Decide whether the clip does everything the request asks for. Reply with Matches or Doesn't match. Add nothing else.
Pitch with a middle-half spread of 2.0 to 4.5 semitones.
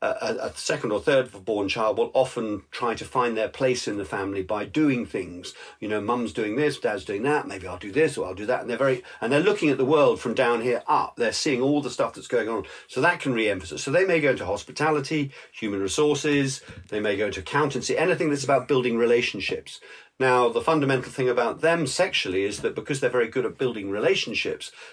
Doesn't match